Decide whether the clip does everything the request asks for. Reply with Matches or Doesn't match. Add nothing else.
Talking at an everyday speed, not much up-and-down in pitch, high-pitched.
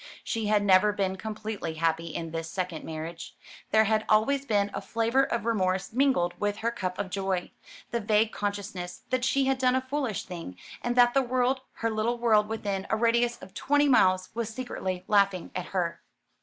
Doesn't match